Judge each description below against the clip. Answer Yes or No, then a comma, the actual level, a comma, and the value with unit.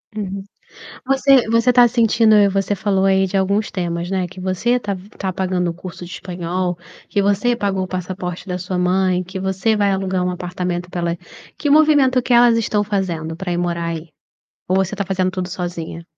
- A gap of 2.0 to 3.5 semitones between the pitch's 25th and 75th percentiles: Yes, narrow, 2.5 semitones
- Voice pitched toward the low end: No, high, 190 Hz